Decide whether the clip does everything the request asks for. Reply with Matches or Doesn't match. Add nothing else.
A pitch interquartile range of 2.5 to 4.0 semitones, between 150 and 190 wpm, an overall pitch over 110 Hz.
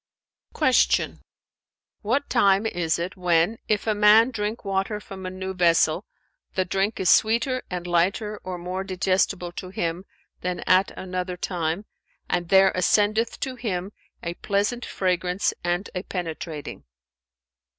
Doesn't match